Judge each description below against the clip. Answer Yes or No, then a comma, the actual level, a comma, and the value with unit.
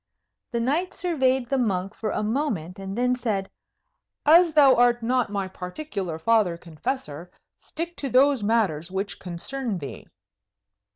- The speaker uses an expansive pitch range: Yes, wide, 6.0 semitones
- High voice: Yes, high, 230 Hz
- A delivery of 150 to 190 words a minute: No, average, 140 wpm